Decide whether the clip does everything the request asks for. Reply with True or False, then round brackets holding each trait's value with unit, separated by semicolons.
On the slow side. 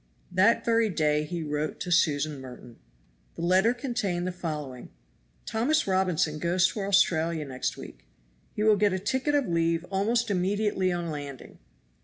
False (155 wpm)